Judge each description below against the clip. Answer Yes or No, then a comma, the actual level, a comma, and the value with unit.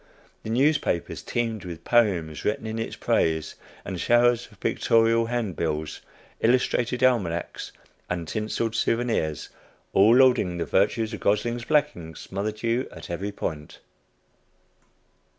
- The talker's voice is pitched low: Yes, low, 110 Hz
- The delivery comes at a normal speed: No, slow, 120 wpm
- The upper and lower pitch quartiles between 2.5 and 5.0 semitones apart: No, wide, 5.4 semitones